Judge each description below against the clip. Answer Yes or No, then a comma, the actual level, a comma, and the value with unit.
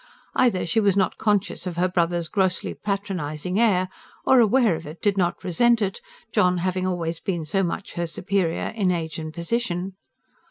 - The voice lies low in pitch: No, medium, 185 Hz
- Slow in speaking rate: No, average, 175 wpm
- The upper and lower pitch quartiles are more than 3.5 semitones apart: No, average, 2.8 semitones